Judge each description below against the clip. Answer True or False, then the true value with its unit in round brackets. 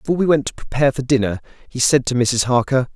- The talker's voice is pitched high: False (130 Hz)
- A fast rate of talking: True (245 wpm)